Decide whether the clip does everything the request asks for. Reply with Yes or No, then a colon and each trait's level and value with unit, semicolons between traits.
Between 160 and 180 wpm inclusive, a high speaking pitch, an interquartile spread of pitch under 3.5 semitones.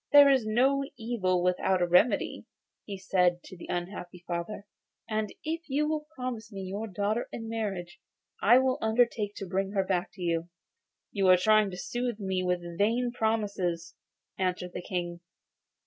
No: average, 165 wpm; high, 200 Hz; average, 4.2 semitones